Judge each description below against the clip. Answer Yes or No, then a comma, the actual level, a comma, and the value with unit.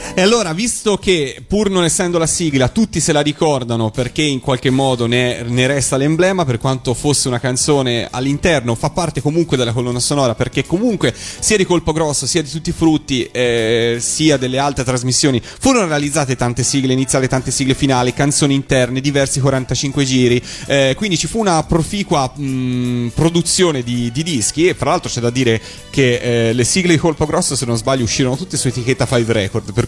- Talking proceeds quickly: Yes, fast, 195 wpm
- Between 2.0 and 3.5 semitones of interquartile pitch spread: No, average, 4.6 semitones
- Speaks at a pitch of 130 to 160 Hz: Yes, low, 135 Hz